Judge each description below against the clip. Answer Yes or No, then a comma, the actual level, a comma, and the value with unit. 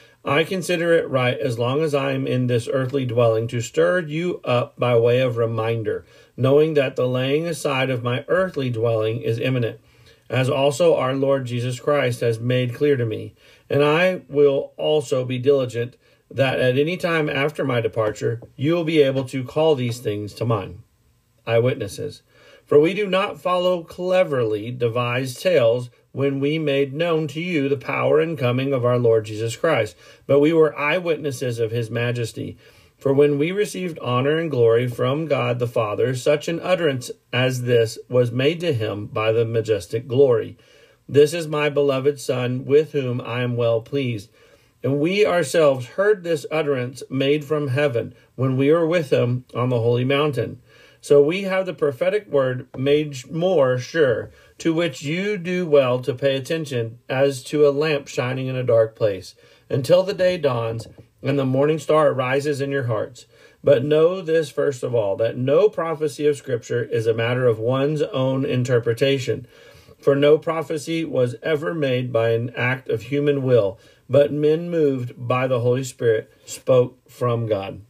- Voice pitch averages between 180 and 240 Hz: No, low, 135 Hz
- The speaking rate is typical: Yes, average, 175 wpm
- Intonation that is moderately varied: Yes, average, 3.8 semitones